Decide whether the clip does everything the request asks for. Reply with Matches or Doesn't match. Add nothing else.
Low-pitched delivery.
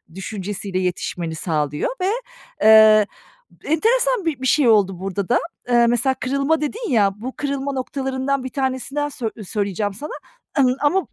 Doesn't match